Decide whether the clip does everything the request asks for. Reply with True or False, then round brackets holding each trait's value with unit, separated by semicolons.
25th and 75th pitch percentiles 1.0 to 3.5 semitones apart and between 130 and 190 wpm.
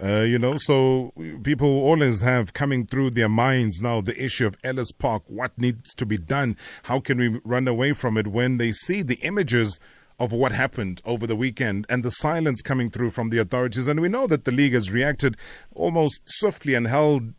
False (2.8 semitones; 205 wpm)